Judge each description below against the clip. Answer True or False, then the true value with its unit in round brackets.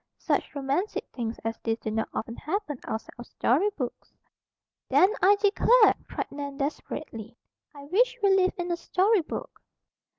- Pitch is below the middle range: False (300 Hz)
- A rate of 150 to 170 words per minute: True (160 wpm)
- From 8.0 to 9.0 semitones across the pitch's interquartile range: True (8.6 semitones)